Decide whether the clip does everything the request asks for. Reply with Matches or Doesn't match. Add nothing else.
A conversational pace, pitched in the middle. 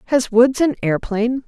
Doesn't match